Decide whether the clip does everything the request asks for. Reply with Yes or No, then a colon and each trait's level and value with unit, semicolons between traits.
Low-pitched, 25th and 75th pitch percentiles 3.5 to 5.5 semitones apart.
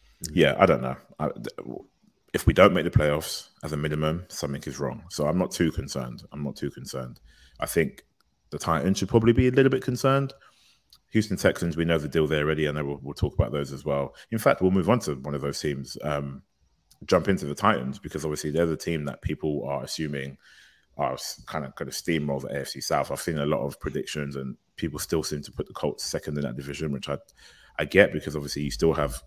No: very low, 75 Hz; average, 2.9 semitones